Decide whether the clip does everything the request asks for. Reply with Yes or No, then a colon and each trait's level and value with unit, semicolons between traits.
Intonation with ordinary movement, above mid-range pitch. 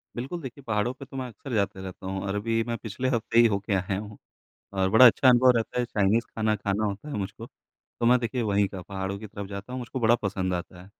No: average, 3.5 semitones; low, 110 Hz